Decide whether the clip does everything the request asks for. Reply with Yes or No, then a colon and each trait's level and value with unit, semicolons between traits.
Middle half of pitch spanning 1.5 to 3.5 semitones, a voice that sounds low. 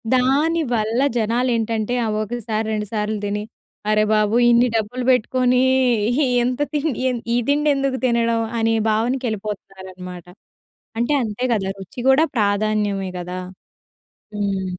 No: average, 3.2 semitones; high, 225 Hz